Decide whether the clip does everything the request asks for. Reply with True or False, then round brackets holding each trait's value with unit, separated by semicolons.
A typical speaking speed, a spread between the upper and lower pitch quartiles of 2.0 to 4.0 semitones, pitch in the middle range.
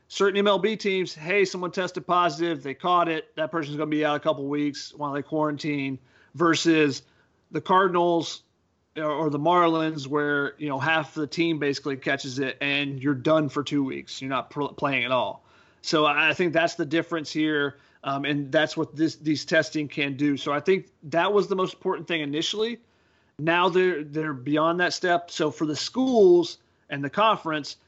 True (185 wpm; 3.1 semitones; 155 Hz)